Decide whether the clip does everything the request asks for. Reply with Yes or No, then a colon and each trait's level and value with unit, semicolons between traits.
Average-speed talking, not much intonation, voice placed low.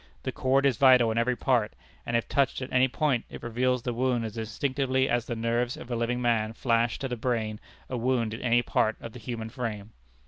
No: fast, 230 wpm; narrow, 1.9 semitones; low, 120 Hz